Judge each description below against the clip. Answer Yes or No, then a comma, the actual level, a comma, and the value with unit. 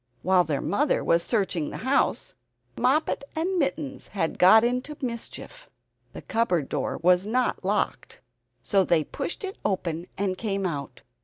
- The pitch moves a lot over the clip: Yes, wide, 7.0 semitones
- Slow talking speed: No, average, 150 wpm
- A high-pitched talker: Yes, high, 205 Hz